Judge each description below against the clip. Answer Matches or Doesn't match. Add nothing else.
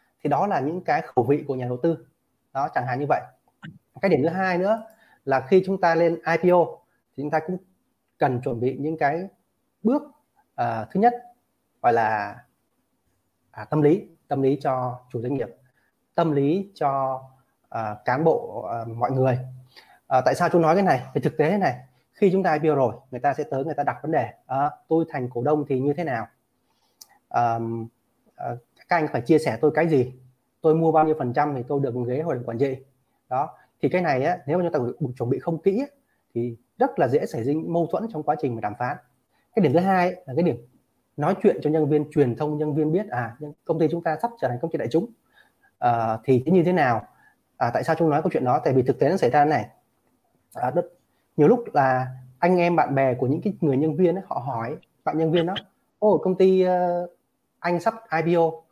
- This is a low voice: Doesn't match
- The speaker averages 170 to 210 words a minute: Doesn't match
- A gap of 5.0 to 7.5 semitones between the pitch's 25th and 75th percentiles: Matches